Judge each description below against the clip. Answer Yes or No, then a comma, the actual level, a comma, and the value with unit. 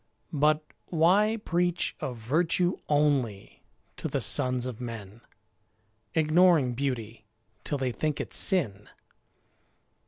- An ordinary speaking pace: No, slow, 105 wpm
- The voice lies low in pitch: No, medium, 145 Hz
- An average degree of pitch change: No, wide, 5.7 semitones